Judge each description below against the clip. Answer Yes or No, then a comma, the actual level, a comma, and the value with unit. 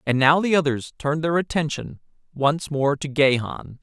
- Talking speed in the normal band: Yes, average, 170 wpm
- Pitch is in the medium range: Yes, medium, 150 Hz